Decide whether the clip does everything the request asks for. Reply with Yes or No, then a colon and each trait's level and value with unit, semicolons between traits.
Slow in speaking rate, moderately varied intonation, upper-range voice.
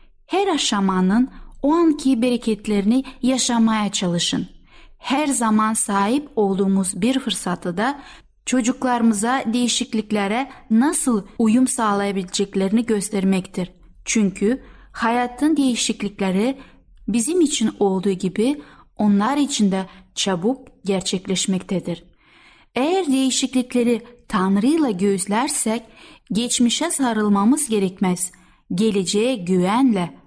Yes: slow, 80 wpm; average, 4.4 semitones; high, 225 Hz